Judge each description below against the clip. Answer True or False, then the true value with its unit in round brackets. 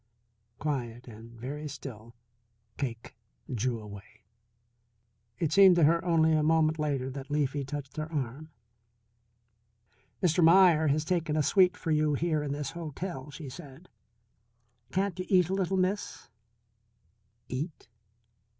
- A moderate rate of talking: False (130 wpm)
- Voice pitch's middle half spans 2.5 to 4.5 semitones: True (4.1 semitones)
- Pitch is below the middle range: False (150 Hz)